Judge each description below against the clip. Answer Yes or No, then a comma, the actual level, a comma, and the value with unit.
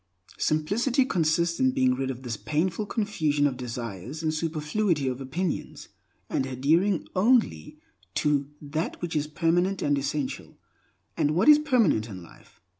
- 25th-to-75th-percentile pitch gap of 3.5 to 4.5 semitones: No, wide, 5.6 semitones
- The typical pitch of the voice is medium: Yes, medium, 155 Hz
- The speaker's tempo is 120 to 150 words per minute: Yes, average, 145 wpm